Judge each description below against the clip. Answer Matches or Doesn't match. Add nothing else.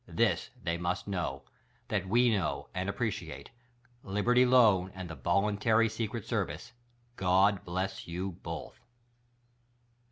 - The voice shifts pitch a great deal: Doesn't match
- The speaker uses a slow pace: Matches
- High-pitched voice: Doesn't match